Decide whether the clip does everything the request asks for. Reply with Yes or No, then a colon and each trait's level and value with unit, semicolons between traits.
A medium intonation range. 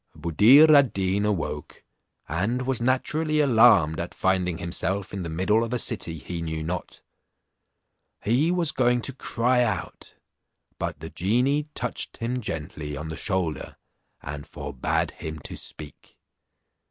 No: wide, 7.4 semitones